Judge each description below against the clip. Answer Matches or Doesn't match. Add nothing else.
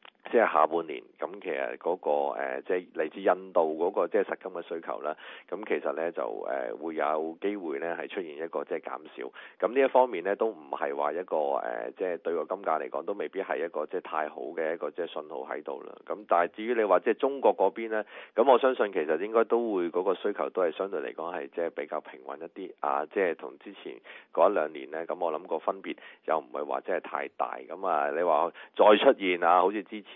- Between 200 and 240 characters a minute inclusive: Doesn't match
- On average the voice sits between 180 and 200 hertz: Doesn't match